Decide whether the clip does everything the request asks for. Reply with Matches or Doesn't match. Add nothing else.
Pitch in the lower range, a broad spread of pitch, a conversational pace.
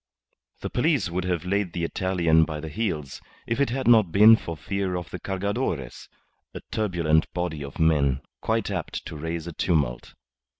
Doesn't match